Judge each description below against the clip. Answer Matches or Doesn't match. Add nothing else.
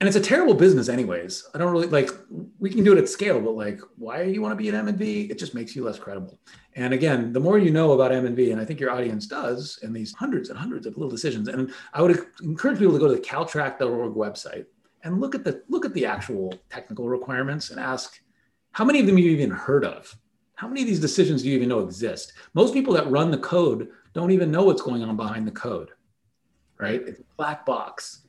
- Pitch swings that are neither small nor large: Doesn't match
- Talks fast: Matches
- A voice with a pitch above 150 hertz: Doesn't match